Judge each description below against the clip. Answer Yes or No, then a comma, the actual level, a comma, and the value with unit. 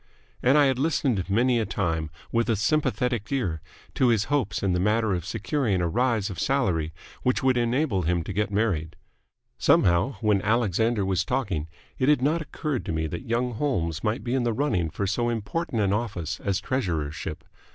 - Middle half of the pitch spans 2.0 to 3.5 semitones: No, wide, 5.4 semitones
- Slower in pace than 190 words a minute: No, average, 195 wpm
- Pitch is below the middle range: Yes, low, 110 Hz